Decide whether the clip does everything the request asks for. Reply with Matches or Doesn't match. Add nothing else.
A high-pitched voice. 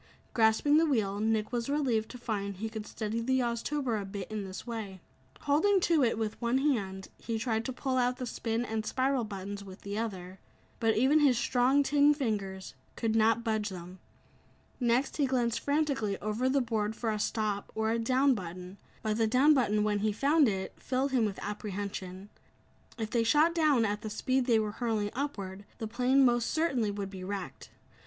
Matches